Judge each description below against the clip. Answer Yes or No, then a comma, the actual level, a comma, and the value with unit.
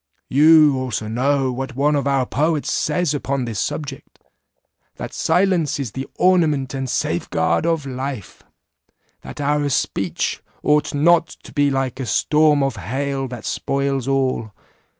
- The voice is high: No, medium, 140 Hz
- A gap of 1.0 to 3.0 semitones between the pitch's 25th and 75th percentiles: Yes, narrow, 2.4 semitones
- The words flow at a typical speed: Yes, average, 150 wpm